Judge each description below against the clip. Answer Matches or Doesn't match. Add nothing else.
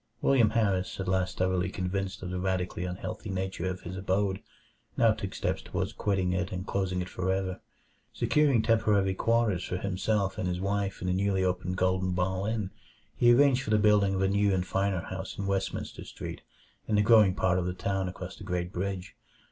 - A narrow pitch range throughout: Matches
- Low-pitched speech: Matches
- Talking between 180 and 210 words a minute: Matches